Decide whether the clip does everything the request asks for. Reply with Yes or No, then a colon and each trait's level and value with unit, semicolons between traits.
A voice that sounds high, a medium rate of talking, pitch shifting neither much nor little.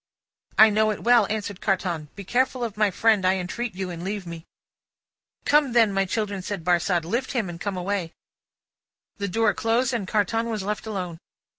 Yes: high, 205 Hz; average, 185 wpm; average, 3.5 semitones